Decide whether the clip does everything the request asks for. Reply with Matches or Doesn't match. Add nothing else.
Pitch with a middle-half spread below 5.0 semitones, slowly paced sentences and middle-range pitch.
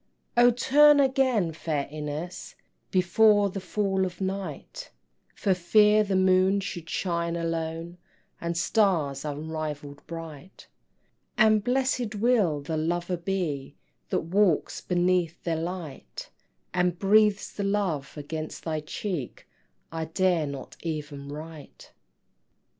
Matches